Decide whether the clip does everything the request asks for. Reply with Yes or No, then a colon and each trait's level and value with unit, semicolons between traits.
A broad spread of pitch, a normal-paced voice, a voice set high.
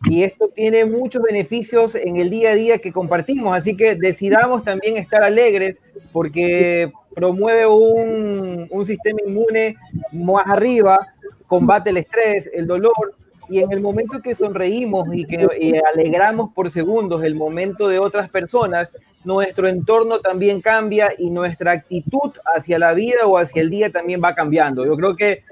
No: average, 3.9 semitones; average, 160 wpm; high, 195 Hz